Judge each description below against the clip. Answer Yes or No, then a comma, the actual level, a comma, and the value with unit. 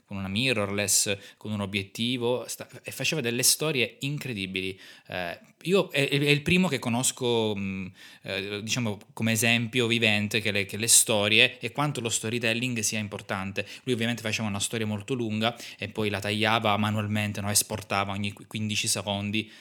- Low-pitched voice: Yes, low, 110 Hz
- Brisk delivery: No, average, 150 wpm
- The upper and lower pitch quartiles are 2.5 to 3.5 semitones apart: Yes, average, 2.8 semitones